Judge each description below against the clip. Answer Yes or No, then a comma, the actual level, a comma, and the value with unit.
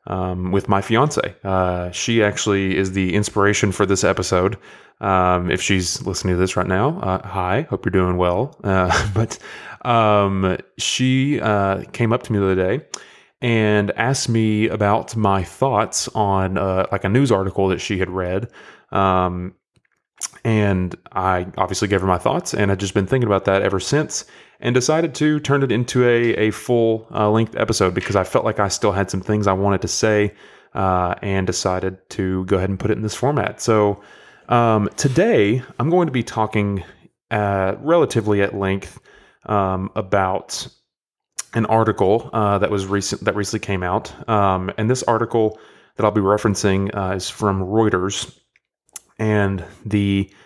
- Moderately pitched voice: No, low, 100 Hz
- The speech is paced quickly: No, average, 175 wpm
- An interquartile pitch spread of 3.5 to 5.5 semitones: No, average, 2.8 semitones